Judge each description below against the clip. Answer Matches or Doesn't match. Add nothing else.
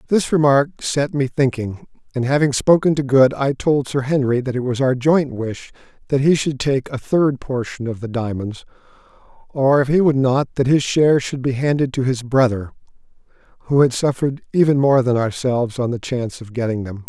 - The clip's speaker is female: Doesn't match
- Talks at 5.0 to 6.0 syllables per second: Matches